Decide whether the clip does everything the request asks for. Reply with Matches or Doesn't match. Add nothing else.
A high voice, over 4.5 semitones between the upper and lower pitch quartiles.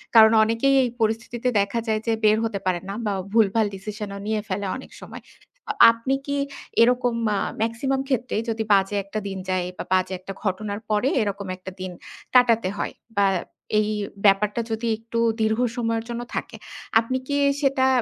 Doesn't match